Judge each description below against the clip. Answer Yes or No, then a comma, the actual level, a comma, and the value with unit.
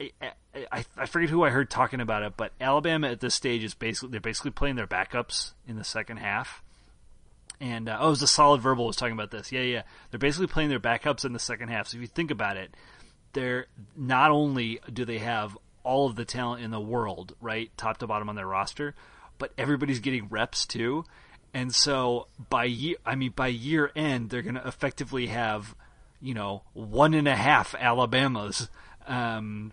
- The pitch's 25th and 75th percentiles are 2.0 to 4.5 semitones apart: Yes, average, 3.4 semitones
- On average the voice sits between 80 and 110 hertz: No, low, 125 Hz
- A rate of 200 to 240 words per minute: Yes, fast, 205 wpm